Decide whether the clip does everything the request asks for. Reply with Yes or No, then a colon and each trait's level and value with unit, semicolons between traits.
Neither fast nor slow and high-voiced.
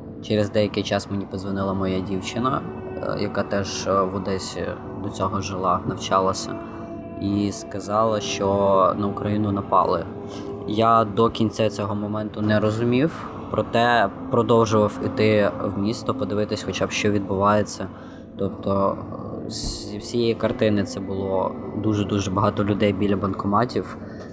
No: average, 125 wpm; low, 100 Hz